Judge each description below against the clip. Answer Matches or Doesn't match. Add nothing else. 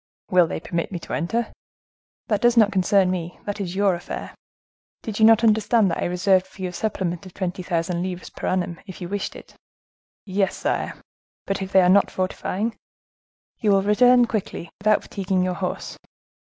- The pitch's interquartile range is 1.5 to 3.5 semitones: Matches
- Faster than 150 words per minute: Matches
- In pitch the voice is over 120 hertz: Matches